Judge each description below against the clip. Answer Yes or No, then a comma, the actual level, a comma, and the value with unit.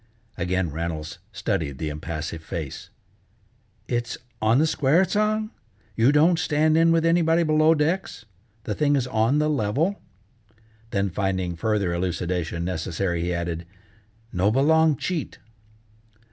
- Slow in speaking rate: Yes, slow, 130 wpm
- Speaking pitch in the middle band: No, low, 110 Hz